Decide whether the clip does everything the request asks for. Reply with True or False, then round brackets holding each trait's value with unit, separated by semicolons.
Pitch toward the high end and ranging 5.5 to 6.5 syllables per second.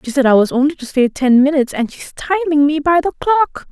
True (290 Hz; 5.7 syllables/s)